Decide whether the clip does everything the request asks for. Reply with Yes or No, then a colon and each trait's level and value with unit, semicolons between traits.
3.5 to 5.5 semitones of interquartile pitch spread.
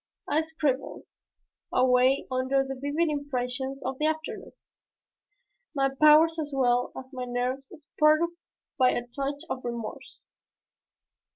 No: average, 2.9 semitones